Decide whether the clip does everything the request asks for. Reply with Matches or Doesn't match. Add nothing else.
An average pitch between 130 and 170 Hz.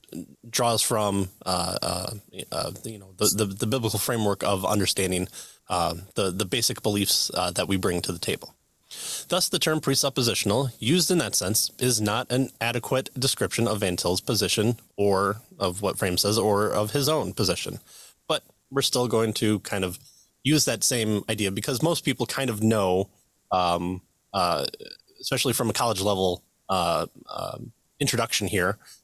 Doesn't match